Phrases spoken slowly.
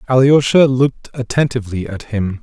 Yes: slow, 125 wpm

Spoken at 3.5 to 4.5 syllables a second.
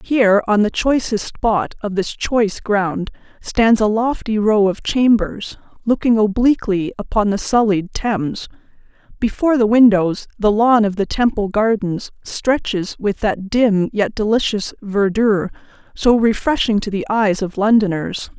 Yes: 4.4 syllables/s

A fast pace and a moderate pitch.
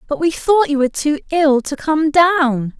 No: fast, 215 wpm; very high, 300 Hz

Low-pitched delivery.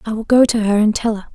No: high, 220 Hz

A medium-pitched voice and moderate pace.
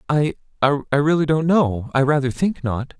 Yes: medium, 145 Hz; average, 160 wpm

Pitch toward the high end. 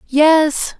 Yes: very high, 305 Hz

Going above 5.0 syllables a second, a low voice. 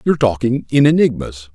Yes: 5.8 syllables/s; low, 125 Hz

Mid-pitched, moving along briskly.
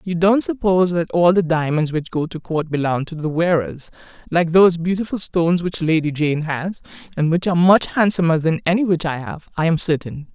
Yes: medium, 170 Hz; fast, 210 wpm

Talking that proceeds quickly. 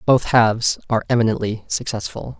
No: slow, 125 wpm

